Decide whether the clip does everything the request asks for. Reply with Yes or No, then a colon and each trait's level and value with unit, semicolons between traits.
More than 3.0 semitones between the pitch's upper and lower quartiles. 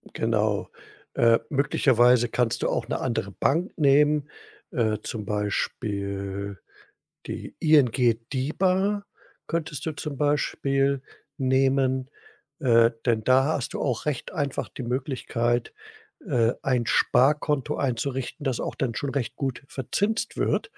Yes: average, 3.7 semitones